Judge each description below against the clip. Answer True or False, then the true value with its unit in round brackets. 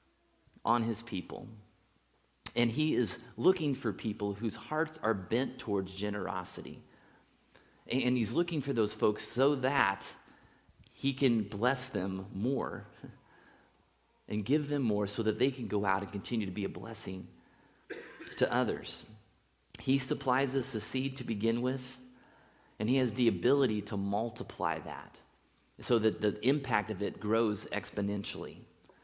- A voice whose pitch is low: True (115 Hz)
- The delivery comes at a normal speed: True (145 wpm)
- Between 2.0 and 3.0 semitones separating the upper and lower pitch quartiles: False (3.7 semitones)